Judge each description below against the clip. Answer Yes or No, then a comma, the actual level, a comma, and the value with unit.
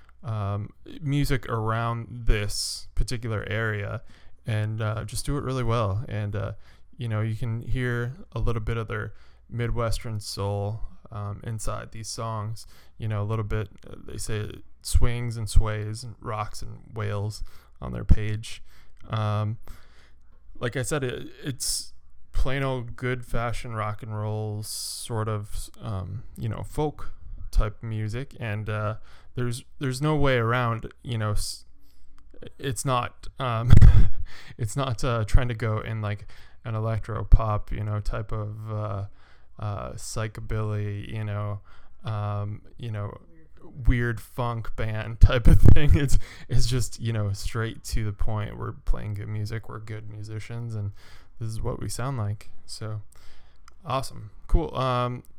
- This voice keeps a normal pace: Yes, average, 150 wpm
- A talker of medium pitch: No, low, 110 Hz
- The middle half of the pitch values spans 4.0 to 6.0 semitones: No, narrow, 2.4 semitones